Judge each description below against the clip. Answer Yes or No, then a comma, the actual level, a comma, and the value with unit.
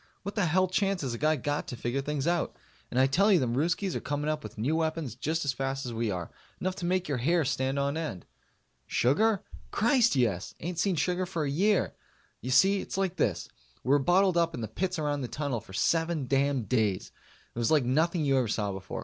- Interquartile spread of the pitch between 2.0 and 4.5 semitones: No, wide, 5.6 semitones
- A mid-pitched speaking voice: Yes, medium, 145 Hz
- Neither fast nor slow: No, fast, 235 wpm